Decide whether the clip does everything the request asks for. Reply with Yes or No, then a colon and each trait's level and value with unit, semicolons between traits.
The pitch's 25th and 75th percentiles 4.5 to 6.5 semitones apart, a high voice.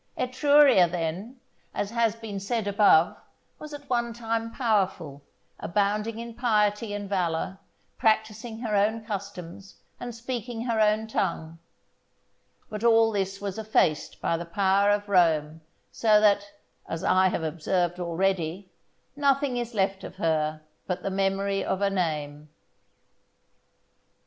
No: average, 3.9 semitones; high, 200 Hz